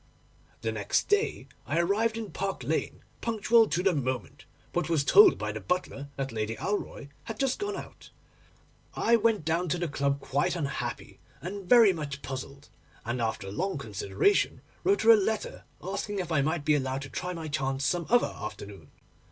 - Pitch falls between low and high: Yes, medium, 170 Hz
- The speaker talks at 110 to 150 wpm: No, average, 180 wpm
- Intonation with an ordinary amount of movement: No, wide, 6.9 semitones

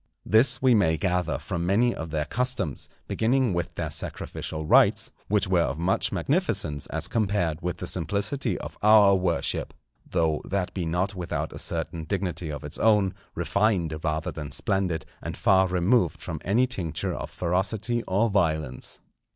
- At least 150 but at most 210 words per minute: Yes, average, 160 wpm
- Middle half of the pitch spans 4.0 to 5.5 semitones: Yes, average, 4.3 semitones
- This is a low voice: Yes, very low, 90 Hz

